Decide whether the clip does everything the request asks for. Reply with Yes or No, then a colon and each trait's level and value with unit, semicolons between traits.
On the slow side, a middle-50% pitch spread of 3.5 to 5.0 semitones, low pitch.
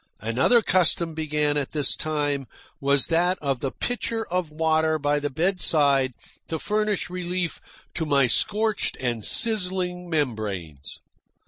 No: slow, 130 wpm; average, 4.5 semitones; medium, 155 Hz